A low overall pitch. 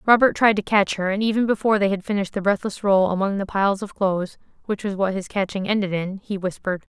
No: high, 200 Hz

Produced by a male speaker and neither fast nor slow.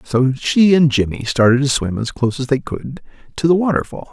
No: male; fast, 220 wpm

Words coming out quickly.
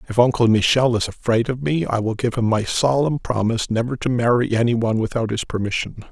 Yes: fast, 215 wpm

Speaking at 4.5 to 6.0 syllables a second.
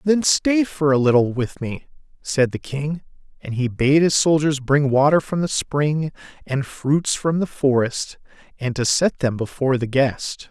No: 4.2 syllables/s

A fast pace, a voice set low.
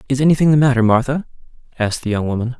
Yes: fast, 210 wpm; low, 130 Hz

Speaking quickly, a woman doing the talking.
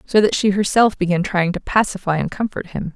Yes: fast, 225 wpm; female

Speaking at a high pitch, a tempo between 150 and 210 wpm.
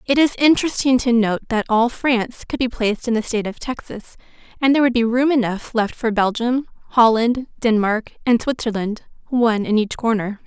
Yes: high, 235 Hz; average, 190 wpm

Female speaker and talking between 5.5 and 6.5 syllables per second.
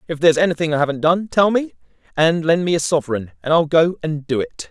No: male; 6.2 syllables/s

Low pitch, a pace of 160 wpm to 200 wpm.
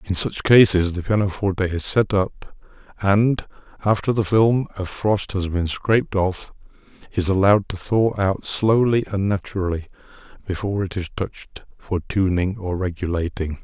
No: very low, 95 Hz; average, 150 wpm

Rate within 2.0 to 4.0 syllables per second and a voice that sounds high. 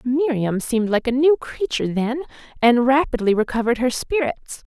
No: 5.3 syllables/s; very high, 255 Hz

